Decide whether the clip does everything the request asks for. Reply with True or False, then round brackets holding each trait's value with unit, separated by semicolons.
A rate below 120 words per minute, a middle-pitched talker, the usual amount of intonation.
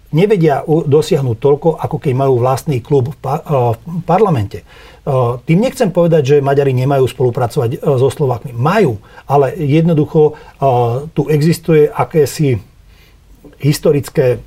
True (110 wpm; 145 Hz; 3.5 semitones)